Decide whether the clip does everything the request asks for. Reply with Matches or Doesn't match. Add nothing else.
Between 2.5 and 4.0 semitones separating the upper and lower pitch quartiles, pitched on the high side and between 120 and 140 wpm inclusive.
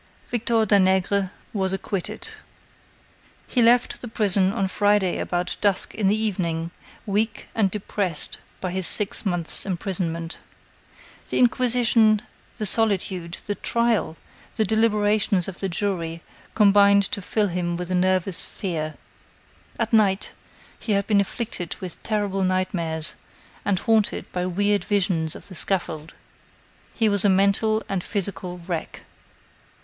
Matches